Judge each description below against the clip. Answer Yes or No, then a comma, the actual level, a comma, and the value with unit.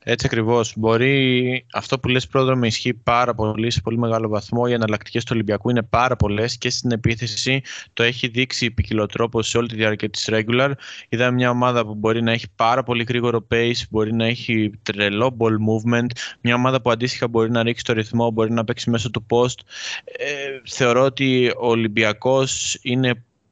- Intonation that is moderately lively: No, narrow, 1.9 semitones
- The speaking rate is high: Yes, fast, 185 wpm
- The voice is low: Yes, low, 120 Hz